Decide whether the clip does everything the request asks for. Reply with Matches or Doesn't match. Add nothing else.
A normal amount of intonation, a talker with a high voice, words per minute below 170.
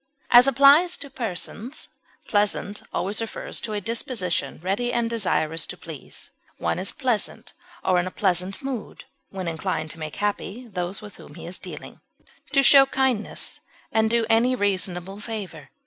Matches